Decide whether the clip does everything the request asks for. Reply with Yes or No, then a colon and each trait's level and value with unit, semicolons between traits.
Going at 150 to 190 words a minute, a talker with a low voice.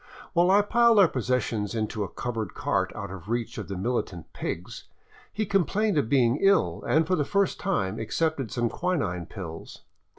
Yes: average, 175 wpm; low, 125 Hz